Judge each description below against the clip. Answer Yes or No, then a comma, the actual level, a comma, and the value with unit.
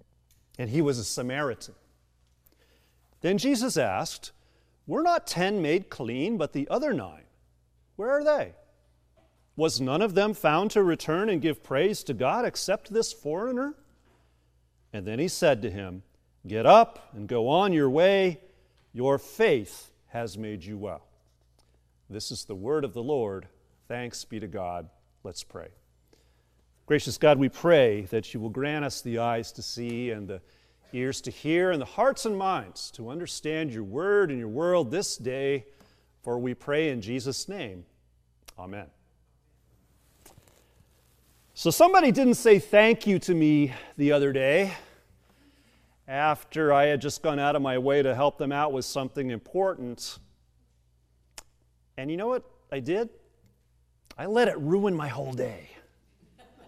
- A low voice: Yes, low, 125 Hz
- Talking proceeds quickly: No, average, 155 wpm